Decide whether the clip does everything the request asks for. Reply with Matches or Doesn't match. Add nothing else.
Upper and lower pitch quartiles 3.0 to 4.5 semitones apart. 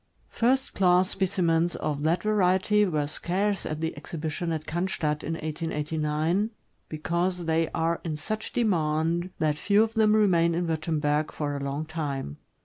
Matches